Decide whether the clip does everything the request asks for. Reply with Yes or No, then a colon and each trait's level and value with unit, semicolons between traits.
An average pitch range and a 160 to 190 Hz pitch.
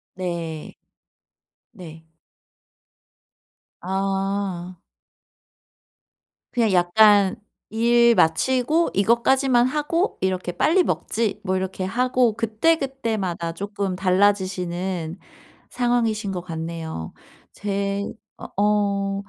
No: average, 4.3 semitones; high, 200 Hz